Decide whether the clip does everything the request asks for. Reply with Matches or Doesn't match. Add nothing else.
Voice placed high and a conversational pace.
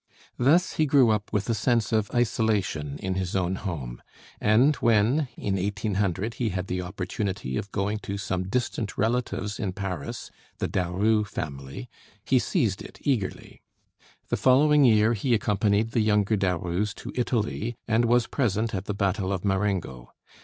Doesn't match